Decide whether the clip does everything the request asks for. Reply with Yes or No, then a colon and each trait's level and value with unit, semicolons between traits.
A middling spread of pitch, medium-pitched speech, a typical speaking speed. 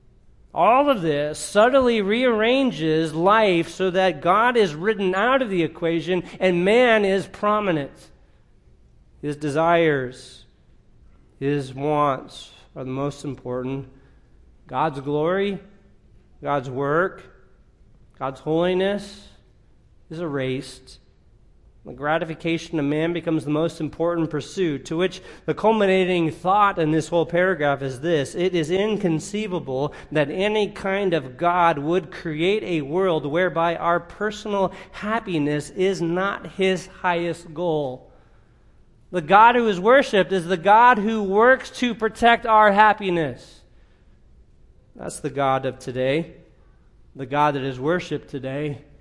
No: average, 4.9 semitones; medium, 170 Hz; slow, 125 wpm